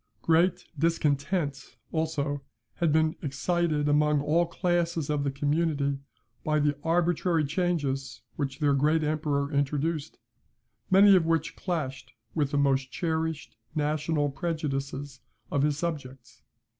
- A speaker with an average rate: No, slow, 120 wpm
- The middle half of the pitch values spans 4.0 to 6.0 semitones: No, average, 2.7 semitones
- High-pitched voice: No, medium, 150 Hz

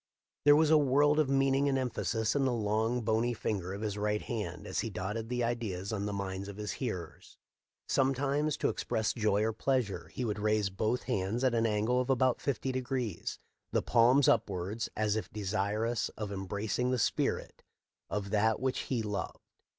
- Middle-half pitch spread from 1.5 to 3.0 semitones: No, average, 3.7 semitones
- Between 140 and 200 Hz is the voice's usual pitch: No, low, 110 Hz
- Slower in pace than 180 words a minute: No, average, 185 wpm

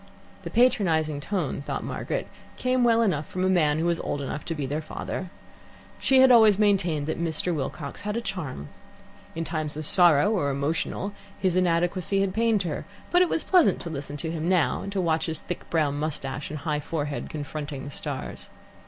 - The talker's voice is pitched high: No, medium, 165 Hz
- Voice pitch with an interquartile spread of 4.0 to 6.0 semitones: Yes, average, 4.8 semitones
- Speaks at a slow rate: No, average, 195 wpm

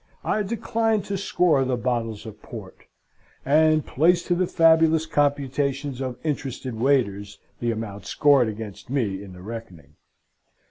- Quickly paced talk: No, average, 140 wpm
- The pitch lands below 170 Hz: Yes, low, 135 Hz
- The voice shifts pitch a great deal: Yes, wide, 6.0 semitones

